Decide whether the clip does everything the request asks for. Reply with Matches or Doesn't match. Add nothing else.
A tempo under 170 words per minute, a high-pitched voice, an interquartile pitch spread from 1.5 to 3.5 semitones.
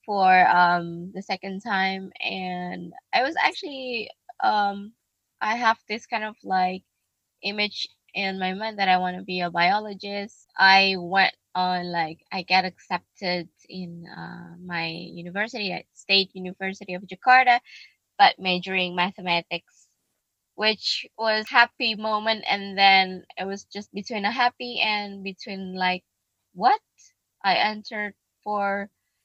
Matches